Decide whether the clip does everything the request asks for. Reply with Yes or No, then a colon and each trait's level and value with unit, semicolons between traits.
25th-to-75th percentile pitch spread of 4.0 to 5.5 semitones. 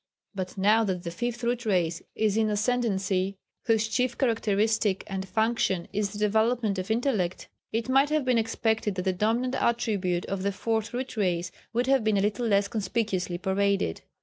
No: average, 3.3 semitones